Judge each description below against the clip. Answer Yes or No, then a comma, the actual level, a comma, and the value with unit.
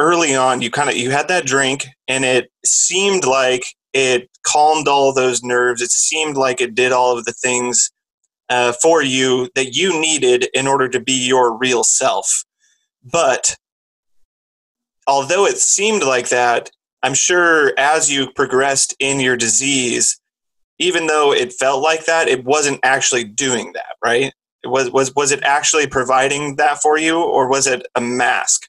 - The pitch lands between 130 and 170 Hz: Yes, low, 135 Hz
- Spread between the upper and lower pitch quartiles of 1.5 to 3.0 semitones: No, average, 3.6 semitones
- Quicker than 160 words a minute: Yes, average, 170 wpm